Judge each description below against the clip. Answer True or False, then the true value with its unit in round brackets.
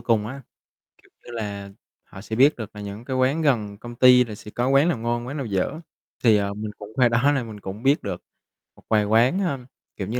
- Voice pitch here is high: False (115 Hz)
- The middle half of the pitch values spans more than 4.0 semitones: False (3.7 semitones)